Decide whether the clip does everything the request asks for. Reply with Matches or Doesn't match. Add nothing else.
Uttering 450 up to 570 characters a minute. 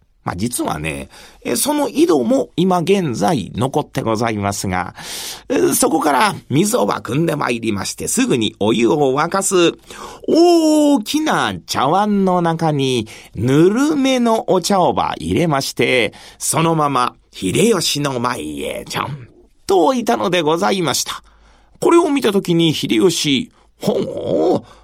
Doesn't match